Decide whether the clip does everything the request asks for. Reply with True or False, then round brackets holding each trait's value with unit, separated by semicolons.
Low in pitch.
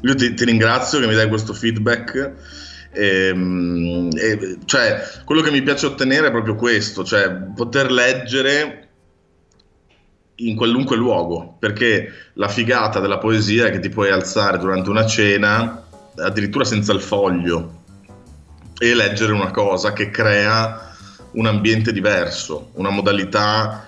True (105 Hz)